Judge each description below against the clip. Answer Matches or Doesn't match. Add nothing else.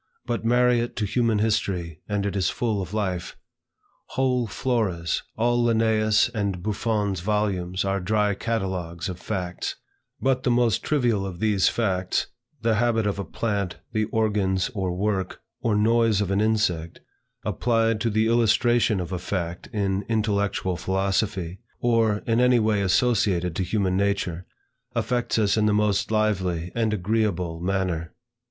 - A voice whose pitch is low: Matches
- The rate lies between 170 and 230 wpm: Doesn't match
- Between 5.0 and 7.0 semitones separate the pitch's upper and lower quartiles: Doesn't match